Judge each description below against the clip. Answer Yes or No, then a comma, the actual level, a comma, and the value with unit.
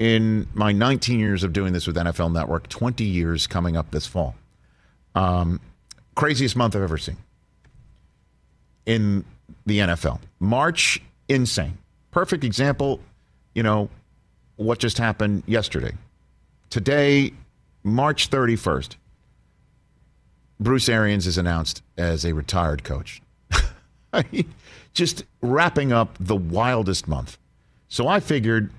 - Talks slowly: Yes, slow, 115 wpm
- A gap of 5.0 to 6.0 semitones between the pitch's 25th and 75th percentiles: Yes, wide, 5.6 semitones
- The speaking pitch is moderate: No, low, 105 Hz